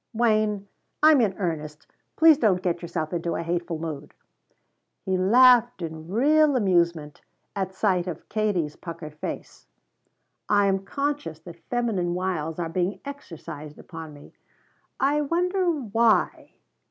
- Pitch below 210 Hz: Yes, high, 190 Hz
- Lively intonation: Yes, wide, 6.3 semitones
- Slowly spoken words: Yes, slow, 130 wpm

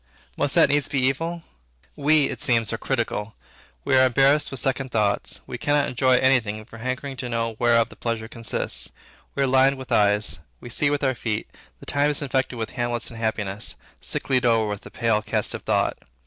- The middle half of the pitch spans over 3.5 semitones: No, average, 3.1 semitones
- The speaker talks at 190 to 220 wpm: Yes, average, 200 wpm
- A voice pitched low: Yes, low, 125 Hz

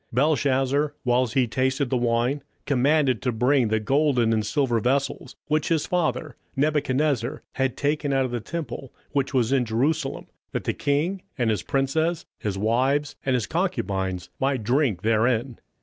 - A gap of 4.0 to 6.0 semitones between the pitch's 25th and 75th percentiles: No, average, 3.6 semitones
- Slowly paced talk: No, average, 165 wpm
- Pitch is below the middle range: Yes, low, 130 Hz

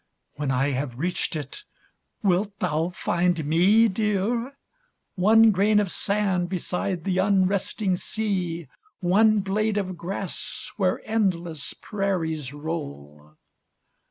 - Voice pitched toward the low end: No, medium, 185 Hz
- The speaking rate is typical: No, slow, 115 wpm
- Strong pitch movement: No, average, 4.1 semitones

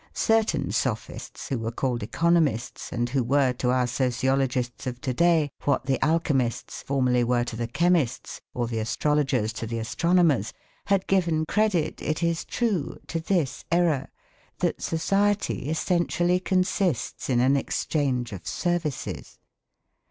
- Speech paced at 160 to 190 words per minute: No, average, 140 wpm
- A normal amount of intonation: No, wide, 5.7 semitones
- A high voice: No, medium, 140 Hz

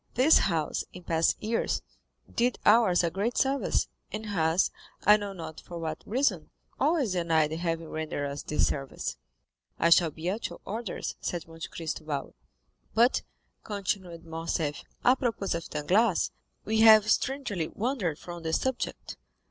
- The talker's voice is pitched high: No, medium, 180 Hz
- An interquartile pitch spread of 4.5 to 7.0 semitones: Yes, average, 5.3 semitones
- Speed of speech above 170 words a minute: No, average, 150 wpm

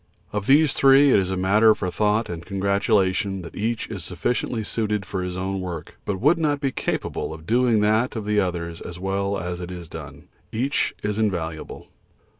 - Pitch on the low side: Yes, low, 100 Hz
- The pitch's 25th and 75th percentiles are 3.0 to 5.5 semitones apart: Yes, average, 3.6 semitones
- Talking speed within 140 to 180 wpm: No, average, 195 wpm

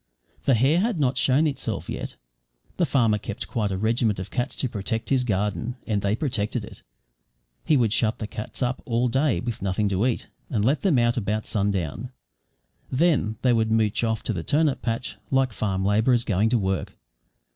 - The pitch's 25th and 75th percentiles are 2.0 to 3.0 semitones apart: No, average, 3.7 semitones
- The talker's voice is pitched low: Yes, low, 115 Hz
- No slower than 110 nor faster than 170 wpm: No, average, 190 wpm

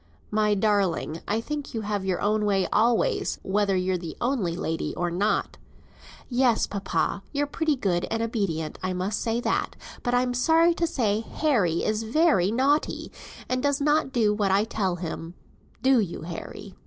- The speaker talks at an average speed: Yes, average, 170 wpm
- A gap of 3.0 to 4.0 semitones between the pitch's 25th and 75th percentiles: No, average, 5.1 semitones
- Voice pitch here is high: Yes, high, 215 Hz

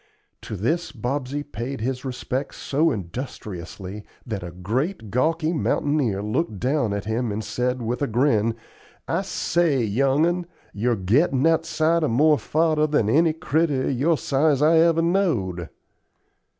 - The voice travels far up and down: Yes, wide, 6.0 semitones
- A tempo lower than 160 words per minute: Yes, average, 150 wpm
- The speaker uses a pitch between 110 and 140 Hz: Yes, low, 135 Hz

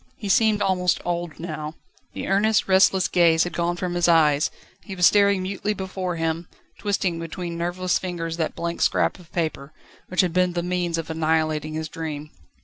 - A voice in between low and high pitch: Yes, medium, 175 Hz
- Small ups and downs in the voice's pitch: Yes, narrow, 2.3 semitones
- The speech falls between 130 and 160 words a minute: No, average, 180 wpm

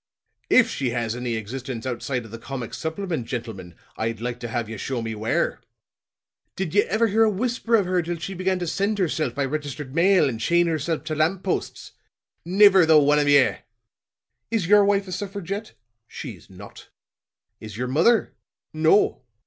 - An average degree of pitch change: No, wide, 7.7 semitones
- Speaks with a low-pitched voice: No, medium, 155 Hz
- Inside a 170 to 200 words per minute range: Yes, average, 180 wpm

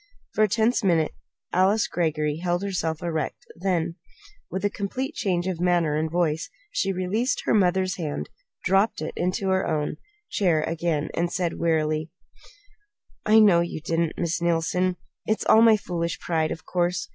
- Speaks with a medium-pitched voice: Yes, medium, 175 Hz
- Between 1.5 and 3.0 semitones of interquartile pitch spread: Yes, average, 2.7 semitones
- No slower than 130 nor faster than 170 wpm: Yes, average, 160 wpm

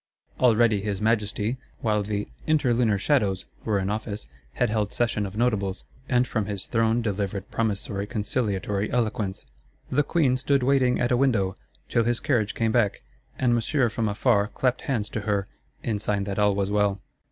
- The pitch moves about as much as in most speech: Yes, average, 3.1 semitones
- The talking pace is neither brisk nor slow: Yes, average, 170 wpm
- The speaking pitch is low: Yes, low, 110 Hz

